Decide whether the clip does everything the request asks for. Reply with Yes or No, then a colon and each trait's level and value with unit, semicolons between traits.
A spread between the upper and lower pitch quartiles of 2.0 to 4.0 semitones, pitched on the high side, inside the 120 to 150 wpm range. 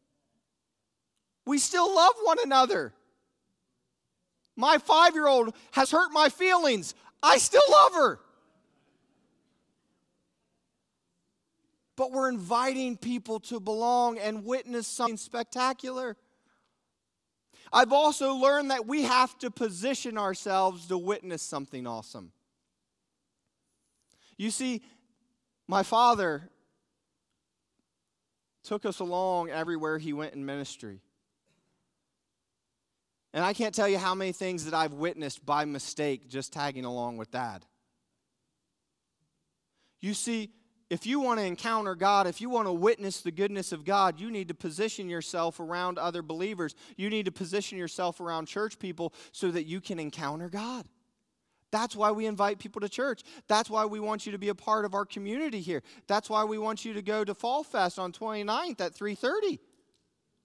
No: wide, 5.4 semitones; high, 215 Hz; average, 140 wpm